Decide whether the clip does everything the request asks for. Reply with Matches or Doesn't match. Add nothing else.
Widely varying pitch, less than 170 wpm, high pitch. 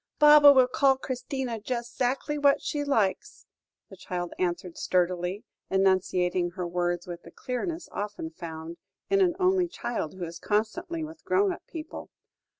Matches